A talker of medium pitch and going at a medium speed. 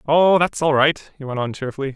No: medium, 145 Hz; fast, 245 wpm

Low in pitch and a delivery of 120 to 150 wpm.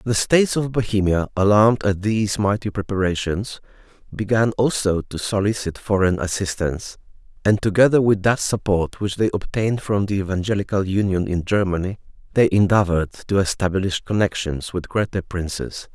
Yes: low, 100 Hz; average, 140 wpm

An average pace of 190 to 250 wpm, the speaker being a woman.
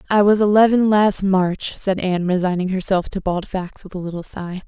Yes: fast, 205 wpm; female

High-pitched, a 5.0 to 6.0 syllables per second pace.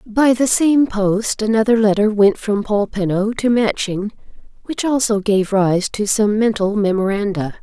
No: high, 210 Hz; 4.3 syllables/s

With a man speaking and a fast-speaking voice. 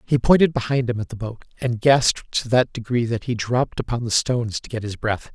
Yes: male; fast, 245 wpm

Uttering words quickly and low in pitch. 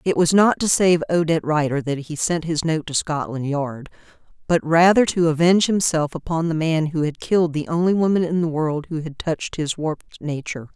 No: fast, 210 wpm; medium, 160 Hz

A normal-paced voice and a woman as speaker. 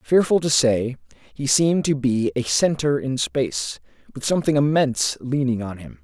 No: average, 170 wpm; male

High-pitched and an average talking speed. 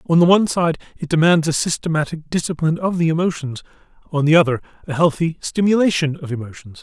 No: medium, 160 Hz; average, 175 wpm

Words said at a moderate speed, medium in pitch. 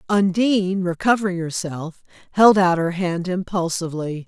No: slow, 110 wpm; medium, 180 Hz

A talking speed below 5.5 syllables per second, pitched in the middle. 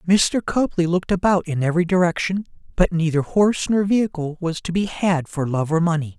No: 5.7 syllables/s; medium, 175 Hz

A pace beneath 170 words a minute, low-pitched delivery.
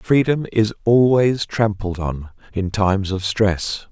Yes: average, 140 wpm; low, 105 Hz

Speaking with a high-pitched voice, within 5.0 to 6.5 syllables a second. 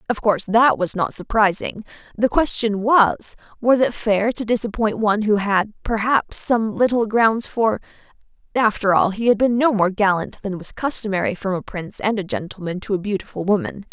Yes: high, 210 Hz; 5.2 syllables/s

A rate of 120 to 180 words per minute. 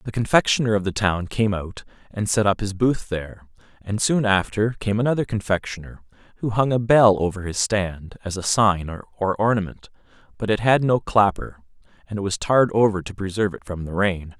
No: average, 195 wpm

